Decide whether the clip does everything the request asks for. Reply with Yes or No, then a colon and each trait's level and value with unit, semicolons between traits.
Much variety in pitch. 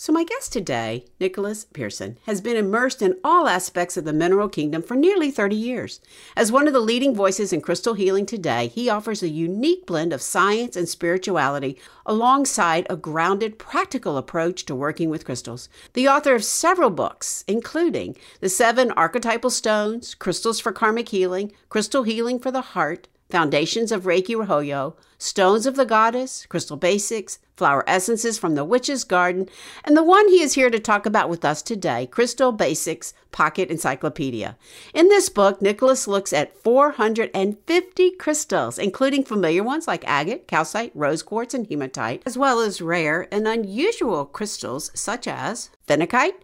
Yes: wide, 6.6 semitones